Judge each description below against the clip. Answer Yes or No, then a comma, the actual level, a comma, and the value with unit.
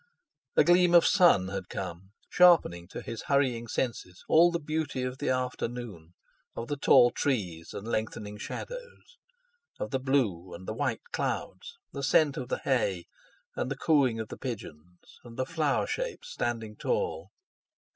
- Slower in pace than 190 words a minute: Yes, average, 160 wpm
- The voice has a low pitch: Yes, low, 125 Hz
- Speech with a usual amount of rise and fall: No, wide, 7.2 semitones